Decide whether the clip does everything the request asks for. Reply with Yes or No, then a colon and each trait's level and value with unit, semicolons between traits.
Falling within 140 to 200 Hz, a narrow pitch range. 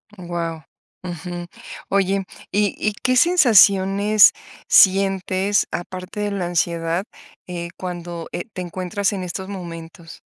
Yes: medium, 185 Hz; narrow, 2.3 semitones